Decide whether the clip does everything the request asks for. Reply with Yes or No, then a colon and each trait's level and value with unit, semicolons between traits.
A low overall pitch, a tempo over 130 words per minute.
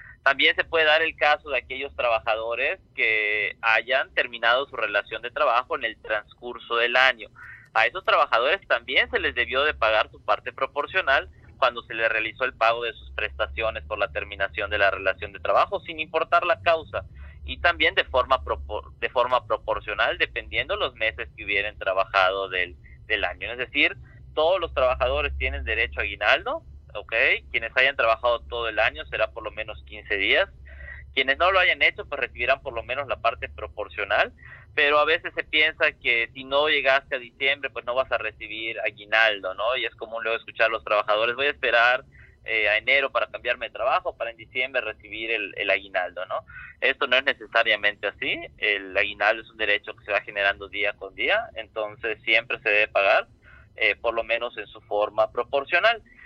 Yes: low, 115 Hz; fast, 190 wpm